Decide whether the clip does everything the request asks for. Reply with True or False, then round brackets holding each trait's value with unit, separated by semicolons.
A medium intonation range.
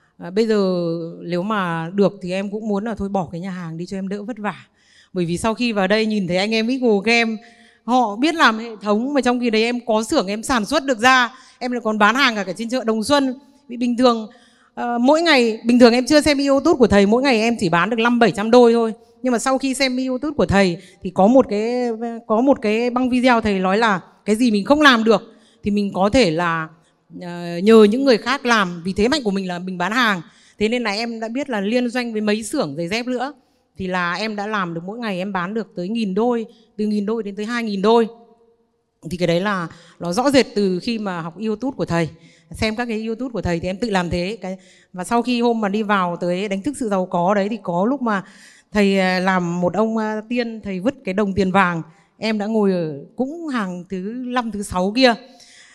True (4.1 semitones)